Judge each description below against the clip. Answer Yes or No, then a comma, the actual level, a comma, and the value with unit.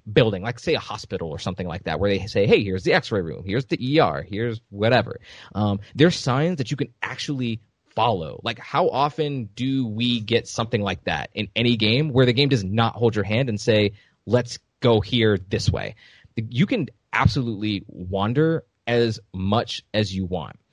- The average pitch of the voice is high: No, low, 115 Hz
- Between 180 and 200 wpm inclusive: Yes, average, 190 wpm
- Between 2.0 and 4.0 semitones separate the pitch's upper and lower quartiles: No, average, 4.4 semitones